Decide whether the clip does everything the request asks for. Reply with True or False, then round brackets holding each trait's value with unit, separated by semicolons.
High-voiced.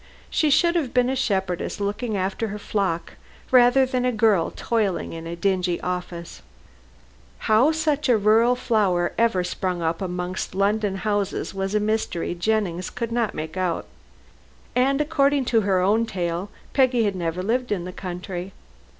True (205 Hz)